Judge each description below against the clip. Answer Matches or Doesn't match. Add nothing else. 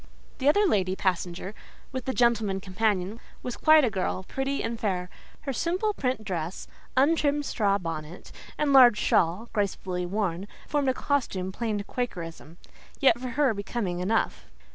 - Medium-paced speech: Matches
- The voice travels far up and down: Matches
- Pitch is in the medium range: Doesn't match